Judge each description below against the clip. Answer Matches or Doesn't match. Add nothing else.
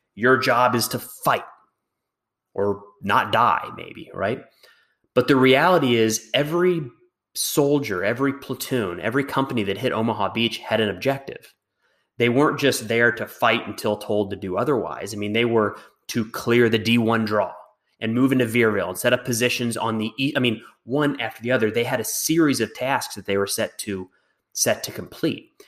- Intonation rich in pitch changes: Doesn't match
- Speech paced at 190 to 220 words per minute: Doesn't match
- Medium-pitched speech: Doesn't match